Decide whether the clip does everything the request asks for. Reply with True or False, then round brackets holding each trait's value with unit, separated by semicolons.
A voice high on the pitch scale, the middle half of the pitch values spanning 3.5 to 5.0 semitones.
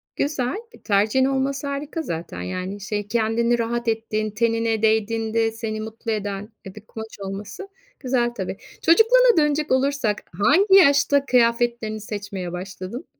True (225 Hz; 4.2 semitones)